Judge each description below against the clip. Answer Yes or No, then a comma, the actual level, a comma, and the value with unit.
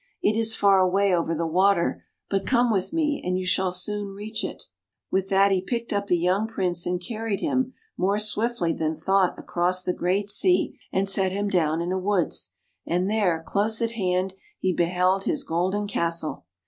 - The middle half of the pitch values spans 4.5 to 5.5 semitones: No, narrow, 2.6 semitones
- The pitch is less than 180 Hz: No, high, 190 Hz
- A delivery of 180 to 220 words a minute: Yes, average, 190 wpm